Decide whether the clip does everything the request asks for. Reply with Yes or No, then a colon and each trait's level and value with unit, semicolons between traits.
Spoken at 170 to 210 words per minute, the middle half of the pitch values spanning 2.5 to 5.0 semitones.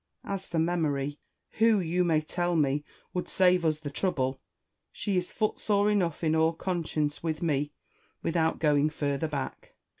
No: average, 155 wpm; average, 3.3 semitones